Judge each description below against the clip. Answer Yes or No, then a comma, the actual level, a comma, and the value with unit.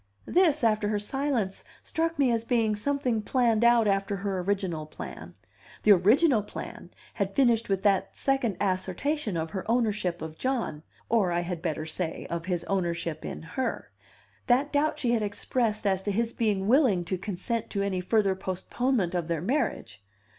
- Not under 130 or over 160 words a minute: No, average, 170 wpm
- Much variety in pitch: No, average, 4.7 semitones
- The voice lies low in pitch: No, high, 205 Hz